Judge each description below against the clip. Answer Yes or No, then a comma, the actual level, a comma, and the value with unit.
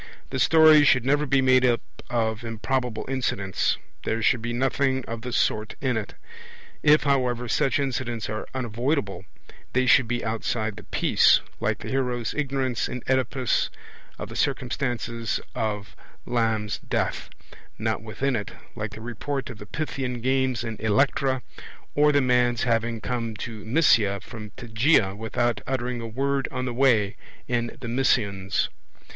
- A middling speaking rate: Yes, average, 150 wpm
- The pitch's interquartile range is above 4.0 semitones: No, average, 2.9 semitones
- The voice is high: No, low, 120 Hz